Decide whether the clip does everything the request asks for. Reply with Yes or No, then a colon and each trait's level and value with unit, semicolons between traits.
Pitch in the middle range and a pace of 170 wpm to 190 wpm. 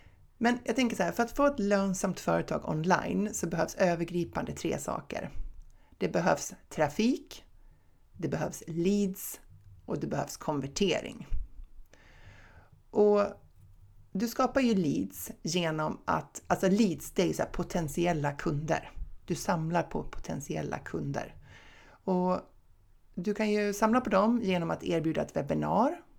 No: medium, 180 Hz; average, 135 wpm